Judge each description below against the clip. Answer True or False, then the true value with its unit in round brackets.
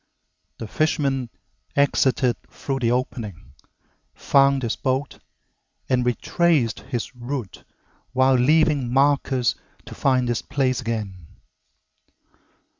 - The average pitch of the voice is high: False (130 Hz)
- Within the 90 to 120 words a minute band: True (100 wpm)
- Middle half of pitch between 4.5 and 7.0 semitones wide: False (2.5 semitones)